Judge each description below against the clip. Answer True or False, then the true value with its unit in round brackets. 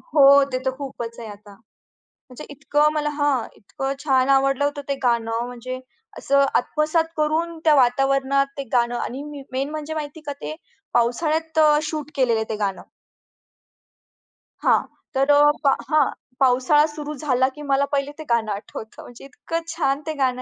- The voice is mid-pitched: False (275 Hz)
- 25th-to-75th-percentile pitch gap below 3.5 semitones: True (3.0 semitones)